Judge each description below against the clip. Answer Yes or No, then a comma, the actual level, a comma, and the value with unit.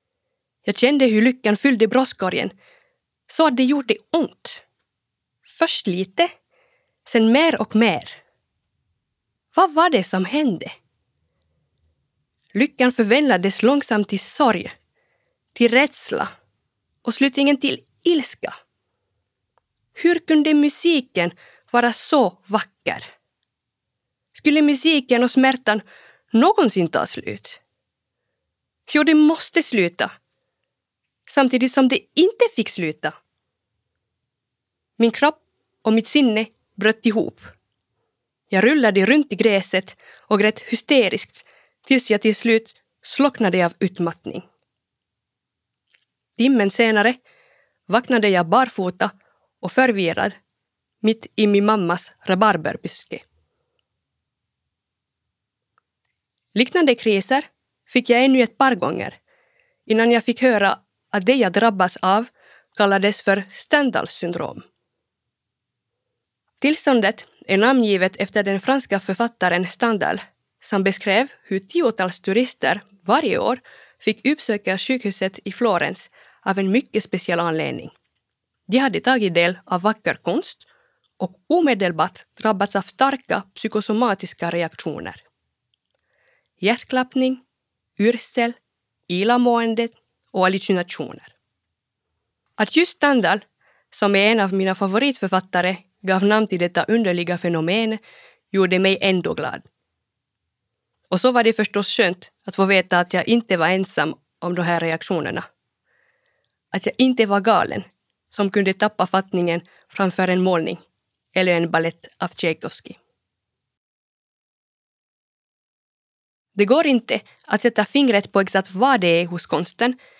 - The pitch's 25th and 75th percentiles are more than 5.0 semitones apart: Yes, wide, 5.5 semitones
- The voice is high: Yes, high, 215 Hz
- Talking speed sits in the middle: No, slow, 110 wpm